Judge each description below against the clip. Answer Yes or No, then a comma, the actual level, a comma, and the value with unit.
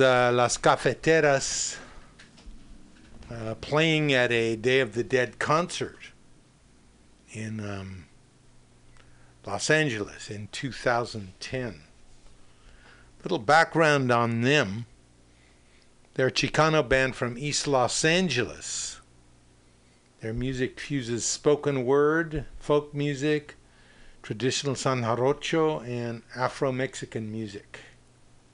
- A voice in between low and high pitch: No, low, 120 Hz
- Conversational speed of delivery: No, slow, 95 wpm